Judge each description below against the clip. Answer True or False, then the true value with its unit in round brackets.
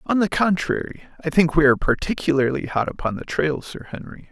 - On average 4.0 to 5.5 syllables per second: False (5.9 syllables/s)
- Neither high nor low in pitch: True (160 Hz)